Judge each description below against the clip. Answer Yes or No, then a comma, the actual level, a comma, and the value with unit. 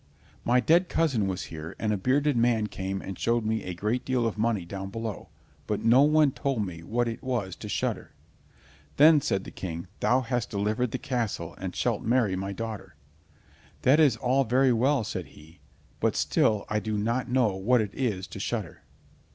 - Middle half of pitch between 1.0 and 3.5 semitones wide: No, average, 4.4 semitones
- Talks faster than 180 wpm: Yes, average, 190 wpm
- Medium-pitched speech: No, low, 115 Hz